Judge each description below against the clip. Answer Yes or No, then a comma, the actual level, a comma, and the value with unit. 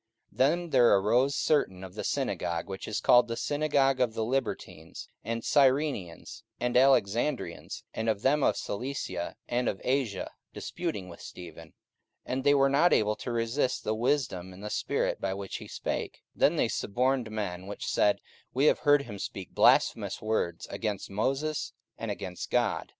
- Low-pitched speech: Yes, low, 115 Hz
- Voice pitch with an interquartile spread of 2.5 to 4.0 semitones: No, wide, 5.5 semitones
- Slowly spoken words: No, average, 175 wpm